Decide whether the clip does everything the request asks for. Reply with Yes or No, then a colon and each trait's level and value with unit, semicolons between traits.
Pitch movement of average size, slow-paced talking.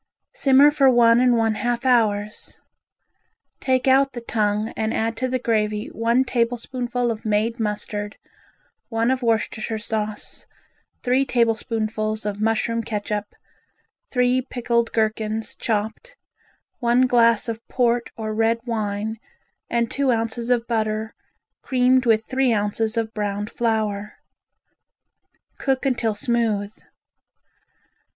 No: narrow, 2.2 semitones; slow, 120 wpm